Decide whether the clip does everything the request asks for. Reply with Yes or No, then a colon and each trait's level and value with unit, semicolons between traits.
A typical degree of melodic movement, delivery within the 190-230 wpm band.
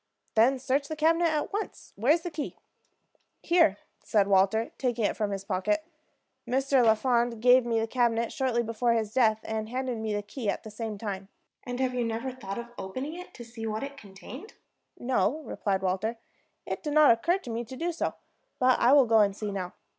Yes: average, 3.6 semitones; fast, 205 wpm